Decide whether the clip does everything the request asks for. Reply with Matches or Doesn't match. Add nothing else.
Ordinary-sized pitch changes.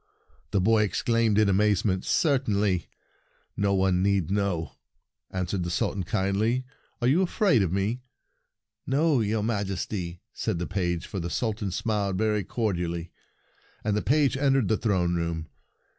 Matches